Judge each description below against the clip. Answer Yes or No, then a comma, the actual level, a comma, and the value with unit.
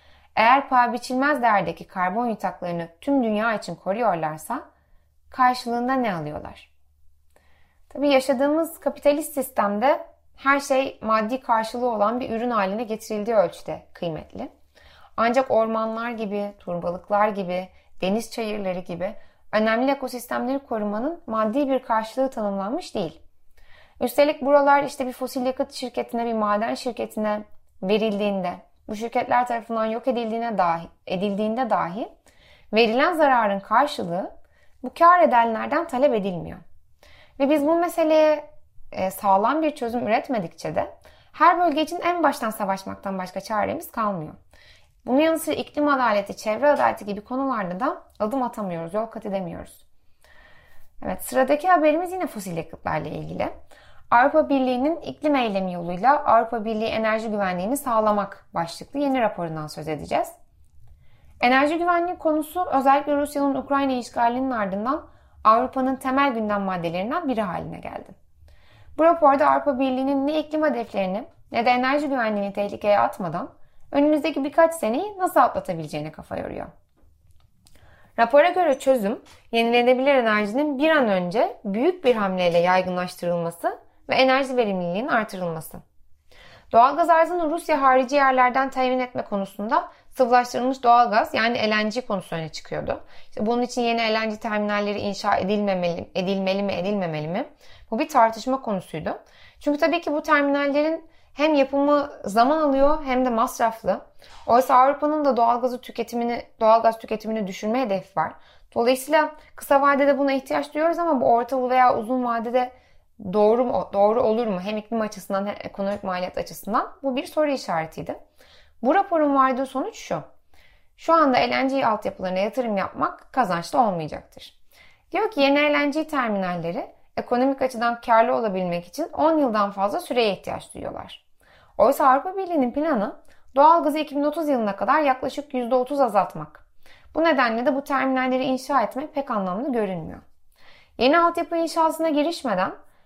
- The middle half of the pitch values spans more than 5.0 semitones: Yes, wide, 5.4 semitones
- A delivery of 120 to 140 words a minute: Yes, average, 130 wpm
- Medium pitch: No, high, 245 Hz